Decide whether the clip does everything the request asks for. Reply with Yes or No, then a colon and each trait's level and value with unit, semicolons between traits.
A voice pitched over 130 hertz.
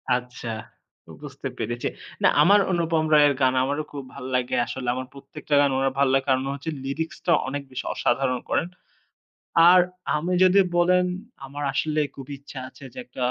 Yes: medium, 140 Hz